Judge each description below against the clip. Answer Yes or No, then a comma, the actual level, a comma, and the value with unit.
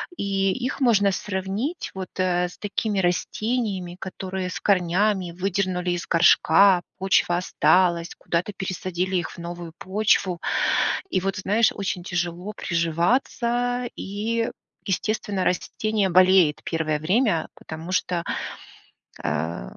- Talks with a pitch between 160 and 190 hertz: Yes, medium, 185 Hz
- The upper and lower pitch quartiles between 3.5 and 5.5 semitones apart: No, average, 2.8 semitones